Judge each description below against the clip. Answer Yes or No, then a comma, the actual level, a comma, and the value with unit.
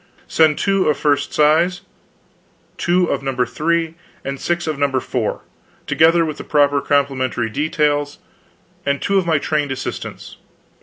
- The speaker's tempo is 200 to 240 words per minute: No, average, 150 wpm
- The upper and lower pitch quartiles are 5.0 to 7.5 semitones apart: No, average, 3.0 semitones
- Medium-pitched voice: Yes, medium, 150 Hz